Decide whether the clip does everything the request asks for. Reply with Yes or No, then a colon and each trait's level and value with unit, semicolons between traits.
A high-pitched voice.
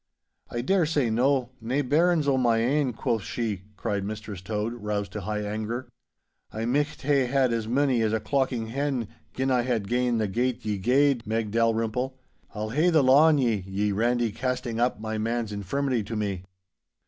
No: low, 120 Hz